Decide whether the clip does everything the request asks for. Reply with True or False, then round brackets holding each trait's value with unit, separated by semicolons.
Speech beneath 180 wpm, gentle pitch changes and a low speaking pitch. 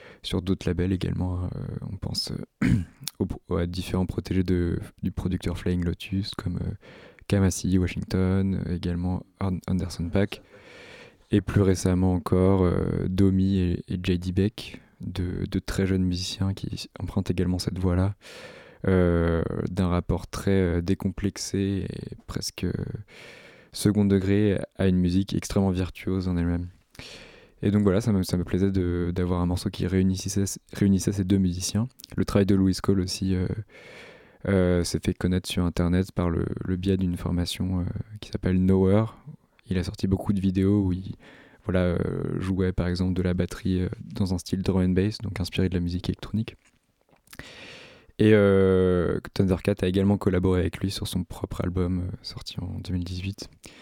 True (160 wpm; 1.5 semitones; 95 Hz)